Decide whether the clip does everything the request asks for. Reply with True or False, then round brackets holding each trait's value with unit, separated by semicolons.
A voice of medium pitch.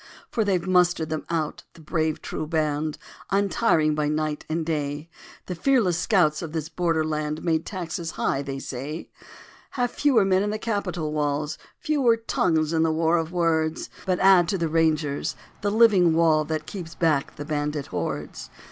True (160 Hz)